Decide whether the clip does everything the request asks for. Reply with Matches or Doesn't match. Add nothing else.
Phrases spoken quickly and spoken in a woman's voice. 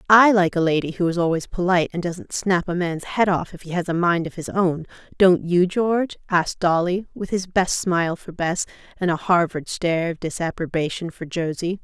Matches